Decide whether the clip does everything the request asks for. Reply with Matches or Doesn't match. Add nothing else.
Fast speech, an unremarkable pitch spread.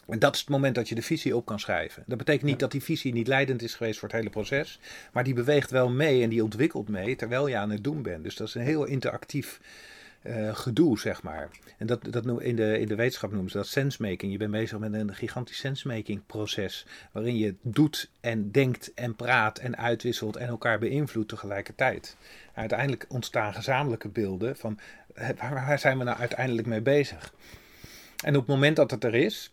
Matches